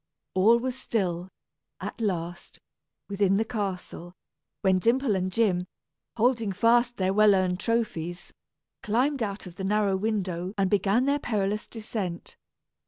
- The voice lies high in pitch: Yes, high, 200 Hz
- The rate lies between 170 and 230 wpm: No, slow, 135 wpm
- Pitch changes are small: No, average, 3.6 semitones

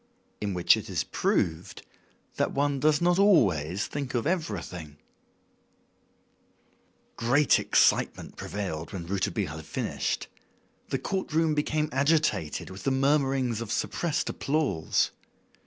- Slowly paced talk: Yes, slow, 120 wpm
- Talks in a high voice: No, low, 130 Hz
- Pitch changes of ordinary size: No, wide, 8.4 semitones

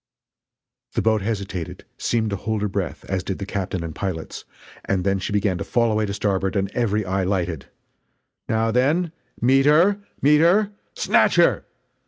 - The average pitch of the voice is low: Yes, low, 105 Hz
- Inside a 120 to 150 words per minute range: No, average, 175 wpm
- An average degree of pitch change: Yes, average, 3.7 semitones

